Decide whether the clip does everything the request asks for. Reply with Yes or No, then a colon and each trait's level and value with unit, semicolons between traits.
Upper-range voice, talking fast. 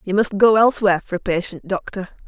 Yes: high, 195 Hz; fast, 210 wpm